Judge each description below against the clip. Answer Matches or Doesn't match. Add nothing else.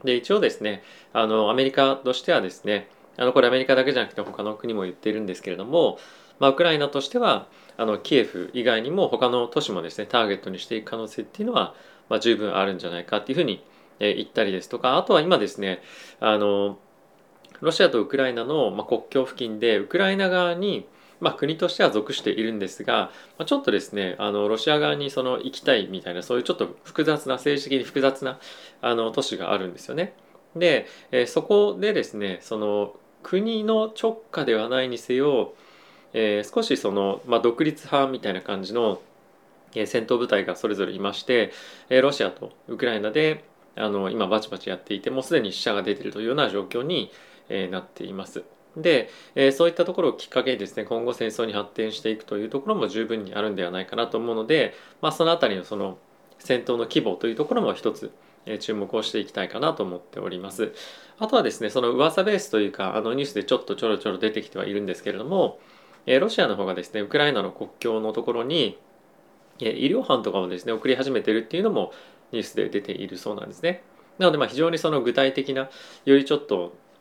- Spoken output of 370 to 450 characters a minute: Matches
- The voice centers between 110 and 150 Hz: Matches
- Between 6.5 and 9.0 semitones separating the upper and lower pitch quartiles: Doesn't match